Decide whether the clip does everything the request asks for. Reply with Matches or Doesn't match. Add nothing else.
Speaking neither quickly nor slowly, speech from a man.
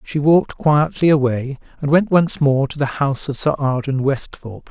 Matches